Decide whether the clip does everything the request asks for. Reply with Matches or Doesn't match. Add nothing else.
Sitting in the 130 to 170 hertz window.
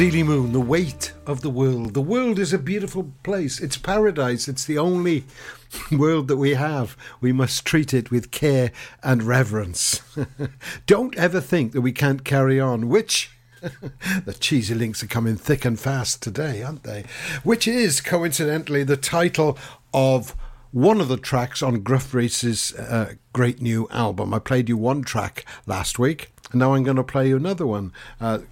Matches